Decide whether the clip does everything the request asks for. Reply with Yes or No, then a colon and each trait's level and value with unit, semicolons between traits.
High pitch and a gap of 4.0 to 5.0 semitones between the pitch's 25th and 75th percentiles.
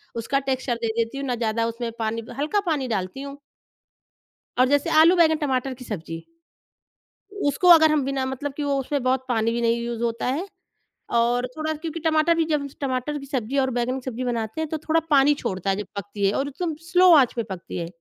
Yes: very high, 260 Hz; average, 4.3 semitones